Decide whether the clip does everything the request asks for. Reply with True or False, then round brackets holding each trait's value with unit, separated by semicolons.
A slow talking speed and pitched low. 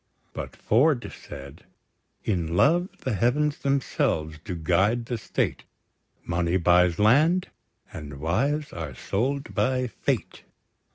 True (115 wpm; 110 Hz)